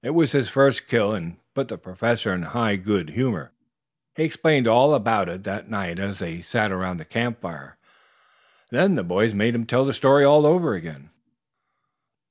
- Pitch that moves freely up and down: Yes, wide, 6.4 semitones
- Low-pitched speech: Yes, low, 110 Hz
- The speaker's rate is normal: Yes, average, 180 wpm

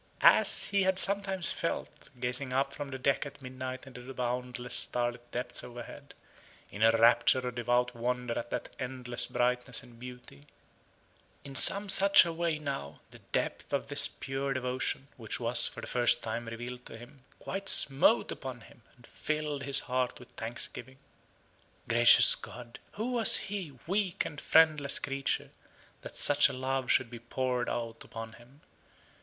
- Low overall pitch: Yes, low, 125 Hz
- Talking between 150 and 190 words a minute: Yes, average, 165 wpm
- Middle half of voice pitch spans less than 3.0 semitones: Yes, narrow, 2.6 semitones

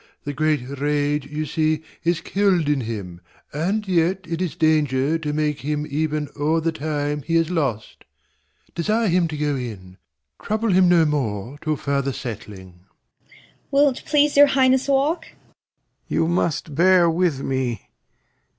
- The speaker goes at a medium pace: Yes, average, 155 wpm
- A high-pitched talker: No, medium, 155 Hz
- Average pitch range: Yes, average, 4.1 semitones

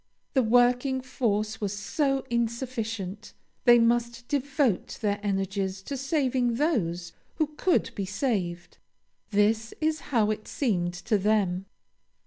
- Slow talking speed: Yes, slow, 120 wpm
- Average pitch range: Yes, average, 4.4 semitones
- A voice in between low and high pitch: No, high, 225 Hz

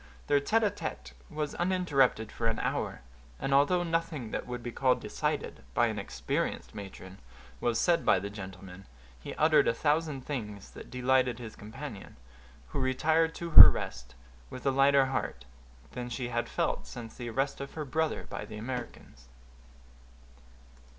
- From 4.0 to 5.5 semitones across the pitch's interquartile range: Yes, average, 5.2 semitones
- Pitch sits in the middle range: No, low, 130 Hz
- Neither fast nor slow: Yes, average, 165 wpm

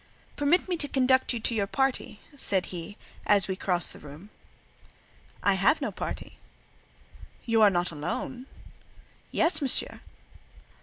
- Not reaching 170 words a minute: Yes, average, 140 wpm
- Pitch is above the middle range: Yes, high, 220 Hz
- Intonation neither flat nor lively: No, wide, 6.5 semitones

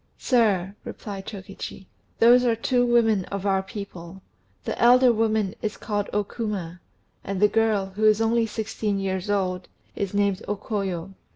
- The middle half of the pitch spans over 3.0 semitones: No, narrow, 2.5 semitones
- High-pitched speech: Yes, high, 205 Hz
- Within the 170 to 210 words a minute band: No, average, 160 wpm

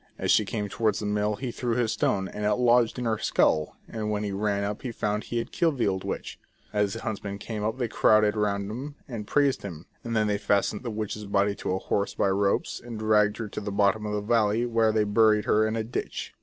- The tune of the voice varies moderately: No, narrow, 1.9 semitones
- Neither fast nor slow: No, fast, 255 wpm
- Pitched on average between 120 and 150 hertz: No, low, 105 Hz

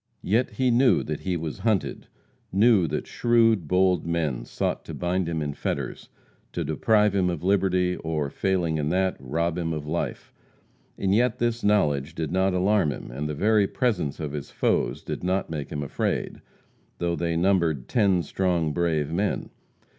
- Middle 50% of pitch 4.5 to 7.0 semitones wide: No, average, 4.1 semitones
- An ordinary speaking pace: Yes, average, 175 wpm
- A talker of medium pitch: No, very low, 90 Hz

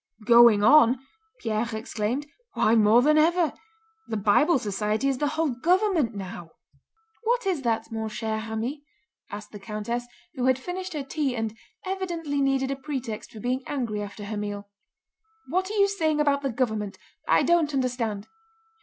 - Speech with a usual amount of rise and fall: No, wide, 5.7 semitones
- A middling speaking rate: Yes, average, 165 wpm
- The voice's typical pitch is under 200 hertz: No, very high, 250 Hz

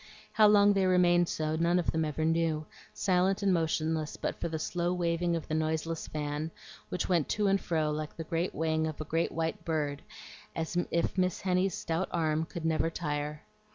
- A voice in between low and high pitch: Yes, medium, 165 Hz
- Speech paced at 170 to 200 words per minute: Yes, average, 190 wpm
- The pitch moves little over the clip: Yes, narrow, 2.2 semitones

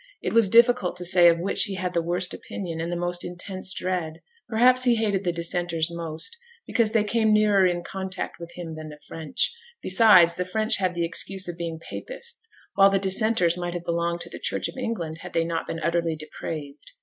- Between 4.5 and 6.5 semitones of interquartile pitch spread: No, average, 3.2 semitones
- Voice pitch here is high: No, medium, 180 Hz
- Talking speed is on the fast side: Yes, fast, 215 wpm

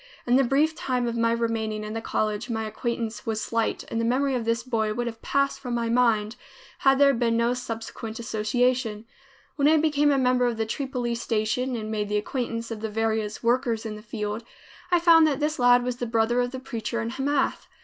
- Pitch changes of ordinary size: No, narrow, 2.3 semitones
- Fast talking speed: Yes, fast, 220 wpm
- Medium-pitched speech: No, high, 235 Hz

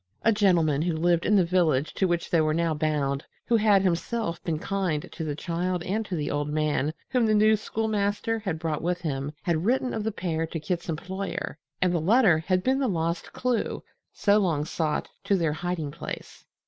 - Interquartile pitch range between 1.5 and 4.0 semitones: No, average, 4.4 semitones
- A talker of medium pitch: Yes, medium, 175 Hz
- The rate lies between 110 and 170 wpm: No, fast, 205 wpm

